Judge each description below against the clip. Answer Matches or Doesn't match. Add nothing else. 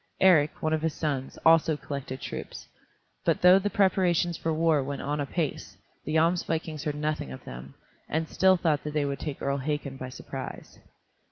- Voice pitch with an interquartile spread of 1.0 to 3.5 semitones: Matches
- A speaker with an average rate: Matches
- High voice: Doesn't match